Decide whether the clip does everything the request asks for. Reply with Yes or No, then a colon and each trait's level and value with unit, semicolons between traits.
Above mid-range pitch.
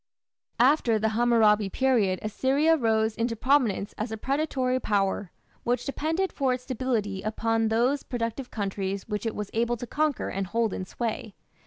Yes: high, 230 Hz